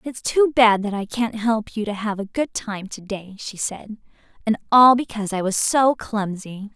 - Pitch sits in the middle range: No, high, 215 Hz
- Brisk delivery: Yes, fast, 215 wpm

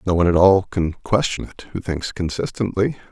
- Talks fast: No, average, 190 wpm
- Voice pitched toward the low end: Yes, very low, 95 Hz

